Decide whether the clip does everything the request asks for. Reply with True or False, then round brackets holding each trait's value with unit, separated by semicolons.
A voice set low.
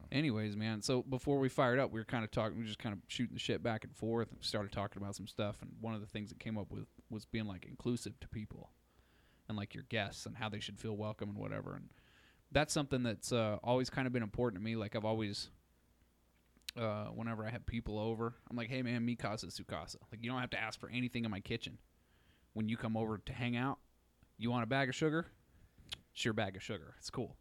True (115 Hz)